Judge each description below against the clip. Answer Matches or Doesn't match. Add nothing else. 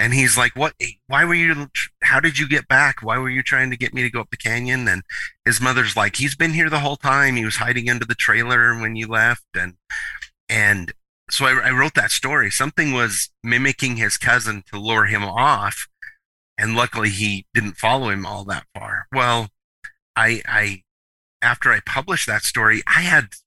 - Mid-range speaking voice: Doesn't match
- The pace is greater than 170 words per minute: Matches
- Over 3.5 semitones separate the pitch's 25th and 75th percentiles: Doesn't match